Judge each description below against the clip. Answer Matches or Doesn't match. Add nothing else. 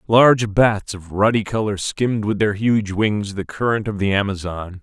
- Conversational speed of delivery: Matches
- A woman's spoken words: Doesn't match